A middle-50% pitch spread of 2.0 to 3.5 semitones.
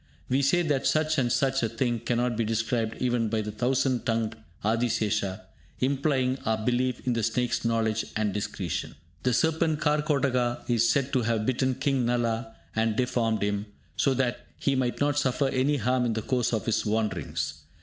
Yes: average, 2.9 semitones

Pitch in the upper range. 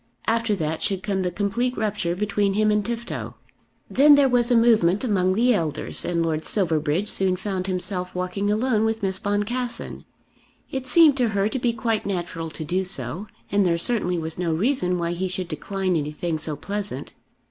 Yes: high, 195 Hz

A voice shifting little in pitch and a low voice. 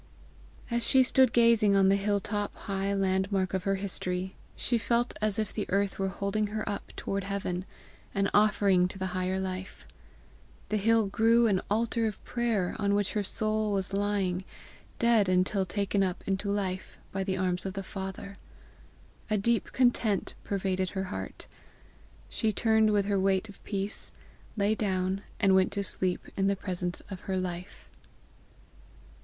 No: narrow, 2.1 semitones; high, 200 Hz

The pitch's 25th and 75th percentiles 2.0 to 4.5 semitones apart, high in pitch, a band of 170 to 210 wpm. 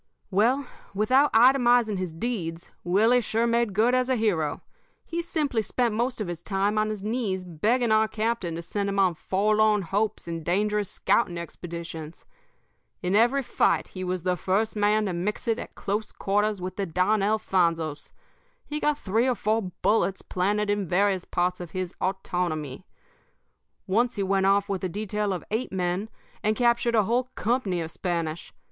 Yes: average, 3.6 semitones; high, 205 Hz; average, 175 wpm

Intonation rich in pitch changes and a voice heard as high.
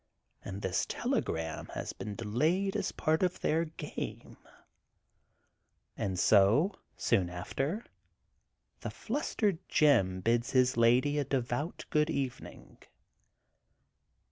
No: wide, 7.6 semitones; low, 130 Hz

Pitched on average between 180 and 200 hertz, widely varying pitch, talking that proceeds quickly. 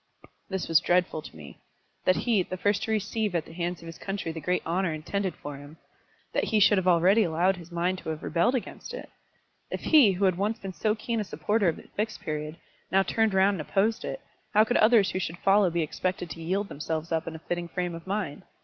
No: medium, 185 Hz; average, 3.7 semitones; fast, 240 wpm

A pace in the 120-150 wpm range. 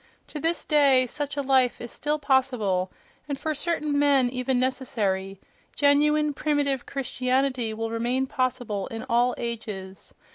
Yes: average, 140 wpm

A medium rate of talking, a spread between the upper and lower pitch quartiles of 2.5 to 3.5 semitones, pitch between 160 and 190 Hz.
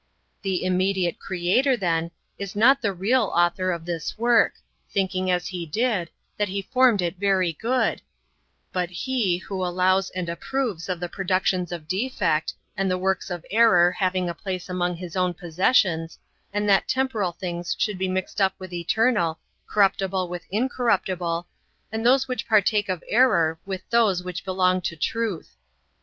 Yes: average, 160 wpm; average, 2.9 semitones; medium, 185 Hz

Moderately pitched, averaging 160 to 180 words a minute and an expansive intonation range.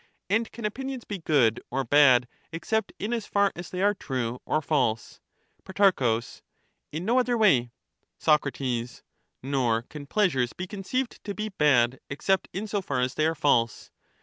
Yes: medium, 160 Hz; average, 170 wpm; wide, 8.0 semitones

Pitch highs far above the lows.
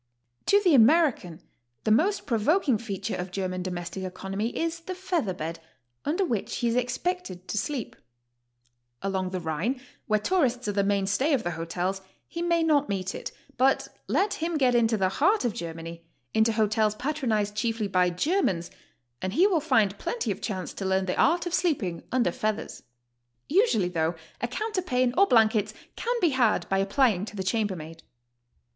Yes: wide, 8.2 semitones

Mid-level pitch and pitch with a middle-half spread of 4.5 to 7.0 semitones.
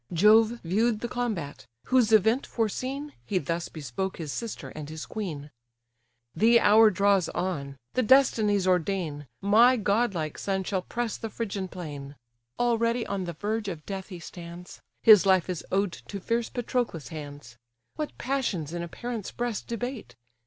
No: high, 200 Hz; average, 5.3 semitones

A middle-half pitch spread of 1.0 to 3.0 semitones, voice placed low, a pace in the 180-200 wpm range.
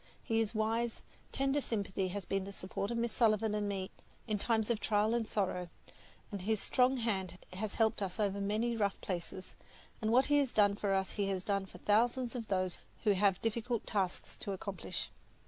No: average, 2.7 semitones; high, 210 Hz; average, 195 wpm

